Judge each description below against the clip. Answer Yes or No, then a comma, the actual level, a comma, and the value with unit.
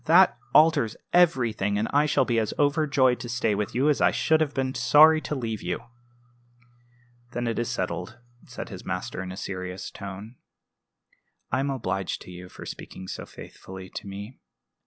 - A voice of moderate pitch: No, low, 120 Hz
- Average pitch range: No, wide, 6.5 semitones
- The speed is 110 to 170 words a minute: No, average, 180 wpm